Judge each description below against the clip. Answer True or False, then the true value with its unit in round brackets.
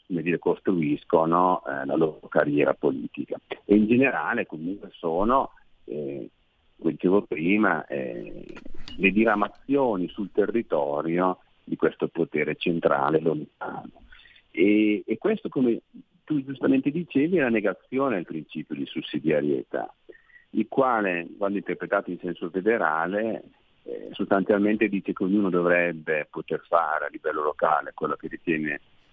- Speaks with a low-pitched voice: True (100 Hz)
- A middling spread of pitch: False (7.6 semitones)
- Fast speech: False (125 wpm)